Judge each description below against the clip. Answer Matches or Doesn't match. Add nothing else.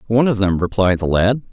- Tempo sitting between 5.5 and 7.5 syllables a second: Matches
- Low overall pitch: Matches